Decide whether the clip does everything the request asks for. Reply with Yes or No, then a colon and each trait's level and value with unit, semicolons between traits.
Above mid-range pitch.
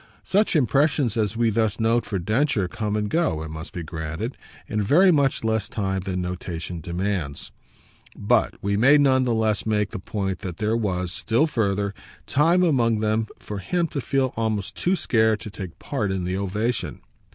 No: low, 110 Hz